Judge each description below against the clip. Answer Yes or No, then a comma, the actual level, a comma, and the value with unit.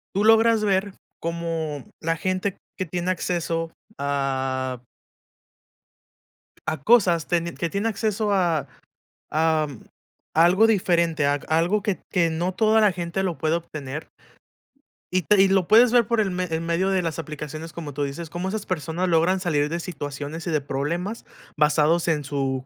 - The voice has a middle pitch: Yes, medium, 170 Hz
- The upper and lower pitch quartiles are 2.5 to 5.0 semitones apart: Yes, average, 3.8 semitones